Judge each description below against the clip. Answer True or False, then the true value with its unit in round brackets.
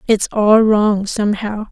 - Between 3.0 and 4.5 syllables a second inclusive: True (4.0 syllables/s)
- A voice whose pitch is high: True (210 Hz)